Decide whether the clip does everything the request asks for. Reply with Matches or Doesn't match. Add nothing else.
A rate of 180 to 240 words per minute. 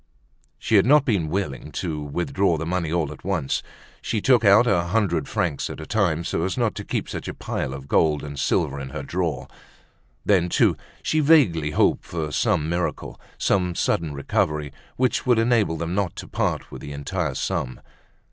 Matches